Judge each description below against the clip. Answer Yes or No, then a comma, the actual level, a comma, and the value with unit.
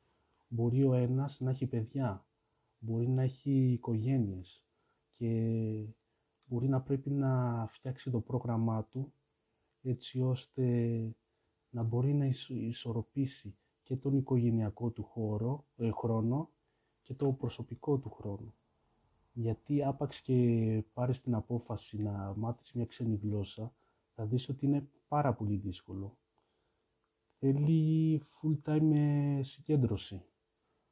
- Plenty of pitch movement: No, average, 3.3 semitones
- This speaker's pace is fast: No, slow, 115 wpm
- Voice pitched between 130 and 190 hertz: No, low, 120 Hz